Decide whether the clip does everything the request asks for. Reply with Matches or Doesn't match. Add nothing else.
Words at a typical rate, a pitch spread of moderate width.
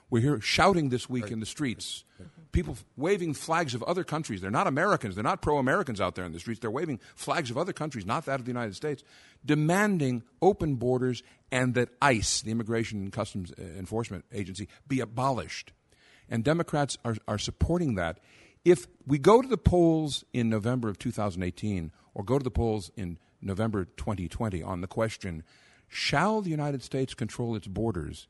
Doesn't match